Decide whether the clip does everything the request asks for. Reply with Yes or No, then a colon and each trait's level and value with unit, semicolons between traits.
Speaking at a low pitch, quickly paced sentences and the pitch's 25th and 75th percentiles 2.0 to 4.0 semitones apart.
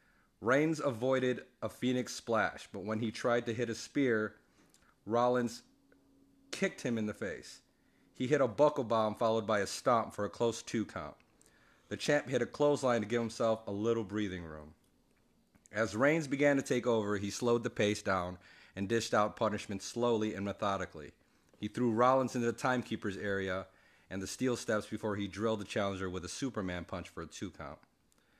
No: low, 110 Hz; average, 185 wpm; average, 3.5 semitones